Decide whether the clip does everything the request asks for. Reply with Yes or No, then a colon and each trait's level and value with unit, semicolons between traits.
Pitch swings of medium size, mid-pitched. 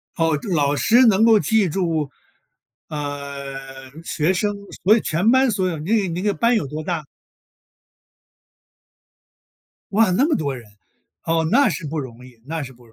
No: wide, 6.6 semitones; medium, 165 Hz